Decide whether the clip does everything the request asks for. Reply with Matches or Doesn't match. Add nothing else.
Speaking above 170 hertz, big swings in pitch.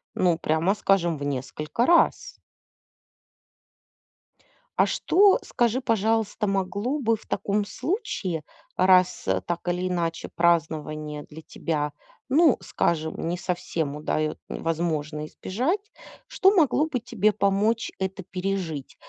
Matches